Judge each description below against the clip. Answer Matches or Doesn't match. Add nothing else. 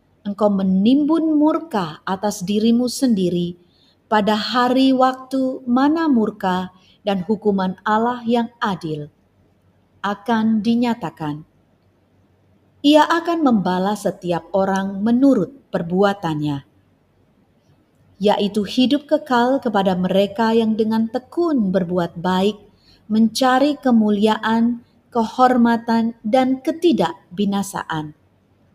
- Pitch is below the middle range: Doesn't match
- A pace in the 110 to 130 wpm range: Doesn't match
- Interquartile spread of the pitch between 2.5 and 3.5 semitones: Doesn't match